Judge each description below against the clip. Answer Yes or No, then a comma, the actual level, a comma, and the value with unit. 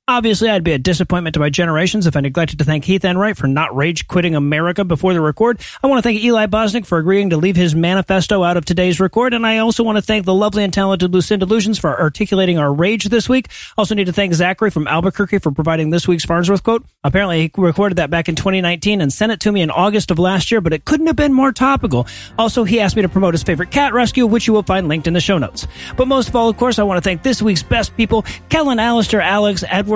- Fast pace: Yes, fast, 260 wpm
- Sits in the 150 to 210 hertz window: Yes, high, 190 Hz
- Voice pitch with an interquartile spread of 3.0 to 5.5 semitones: Yes, average, 4.5 semitones